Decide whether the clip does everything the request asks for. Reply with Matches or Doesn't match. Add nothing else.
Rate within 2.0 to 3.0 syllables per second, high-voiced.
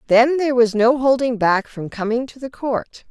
Doesn't match